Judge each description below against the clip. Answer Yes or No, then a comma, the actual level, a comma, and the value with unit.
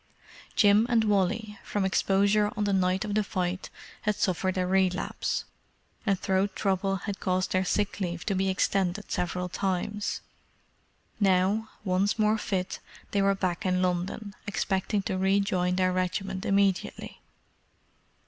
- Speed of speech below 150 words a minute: Yes, average, 140 wpm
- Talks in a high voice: Yes, high, 195 Hz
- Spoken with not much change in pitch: Yes, narrow, 1.8 semitones